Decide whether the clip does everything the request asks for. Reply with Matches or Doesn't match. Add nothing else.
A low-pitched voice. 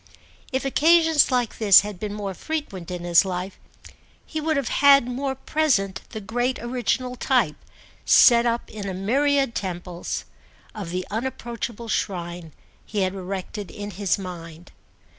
Doesn't match